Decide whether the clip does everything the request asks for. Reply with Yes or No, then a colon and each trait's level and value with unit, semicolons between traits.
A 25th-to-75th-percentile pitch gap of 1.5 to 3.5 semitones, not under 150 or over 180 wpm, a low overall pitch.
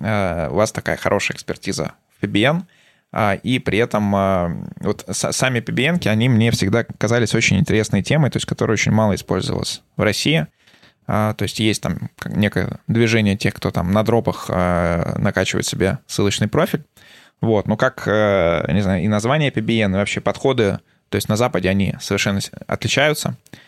Yes: average, 2.8 semitones; average, 155 wpm; low, 105 Hz